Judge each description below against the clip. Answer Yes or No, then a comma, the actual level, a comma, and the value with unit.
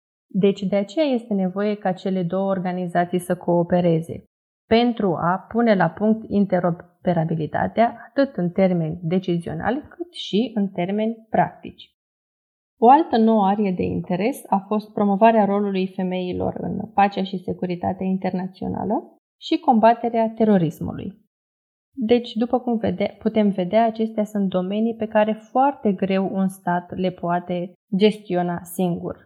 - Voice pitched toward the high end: Yes, high, 200 Hz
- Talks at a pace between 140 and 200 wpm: No, average, 130 wpm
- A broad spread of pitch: No, average, 3.6 semitones